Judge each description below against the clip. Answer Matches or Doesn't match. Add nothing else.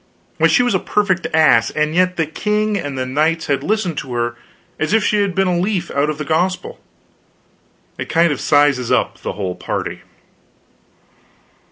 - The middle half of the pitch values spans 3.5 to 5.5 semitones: Matches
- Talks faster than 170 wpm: Matches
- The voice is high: Doesn't match